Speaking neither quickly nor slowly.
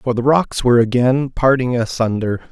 Yes: average, 165 wpm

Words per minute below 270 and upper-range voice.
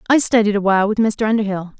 Yes: average, 200 wpm; high, 210 Hz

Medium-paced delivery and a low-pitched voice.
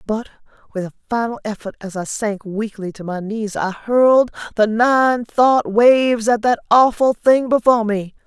No: average, 175 wpm; high, 225 Hz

